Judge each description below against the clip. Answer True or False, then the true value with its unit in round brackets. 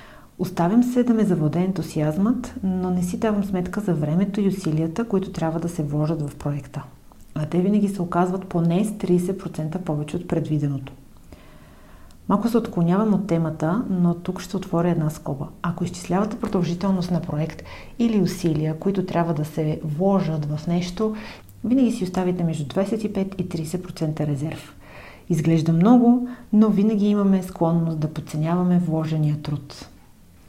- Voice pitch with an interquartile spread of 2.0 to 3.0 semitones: False (3.7 semitones)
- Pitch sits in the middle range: True (175 Hz)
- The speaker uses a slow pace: False (150 wpm)